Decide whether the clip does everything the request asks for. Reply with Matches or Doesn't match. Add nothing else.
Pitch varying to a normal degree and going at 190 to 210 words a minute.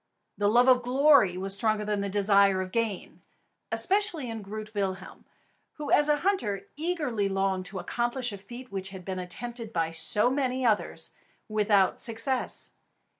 Doesn't match